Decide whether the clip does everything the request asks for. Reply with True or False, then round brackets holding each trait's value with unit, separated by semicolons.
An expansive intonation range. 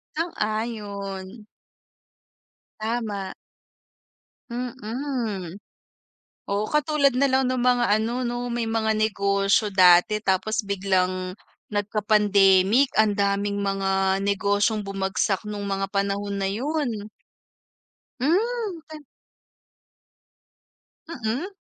False (3.5 semitones)